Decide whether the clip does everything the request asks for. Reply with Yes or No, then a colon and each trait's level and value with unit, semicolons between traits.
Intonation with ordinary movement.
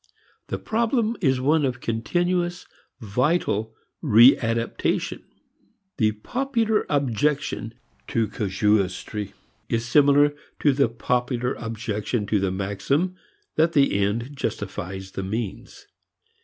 No: wide, 5.7 semitones